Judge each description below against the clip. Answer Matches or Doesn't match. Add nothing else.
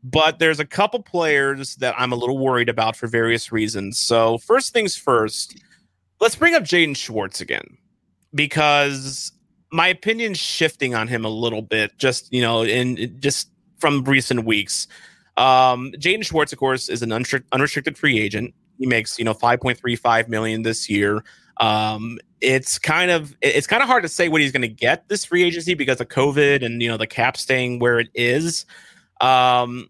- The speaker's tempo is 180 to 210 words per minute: Matches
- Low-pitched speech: Matches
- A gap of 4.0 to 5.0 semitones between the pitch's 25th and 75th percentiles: Doesn't match